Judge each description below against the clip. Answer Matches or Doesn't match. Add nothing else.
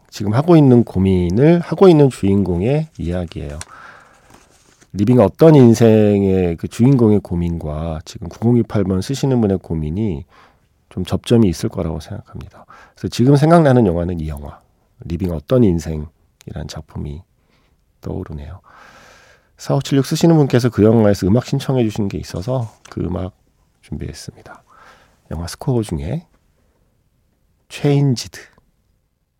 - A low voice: Matches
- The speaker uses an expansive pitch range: Matches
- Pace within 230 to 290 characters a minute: Matches